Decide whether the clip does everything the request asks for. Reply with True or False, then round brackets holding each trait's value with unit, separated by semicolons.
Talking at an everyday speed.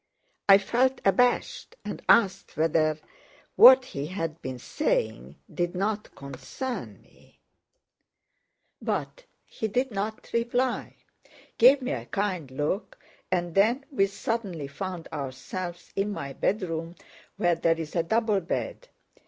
False (125 wpm)